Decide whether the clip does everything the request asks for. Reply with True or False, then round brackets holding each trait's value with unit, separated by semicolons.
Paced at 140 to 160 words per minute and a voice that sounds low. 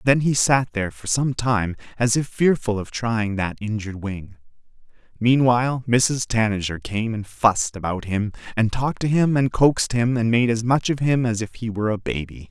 False (200 wpm; 115 Hz)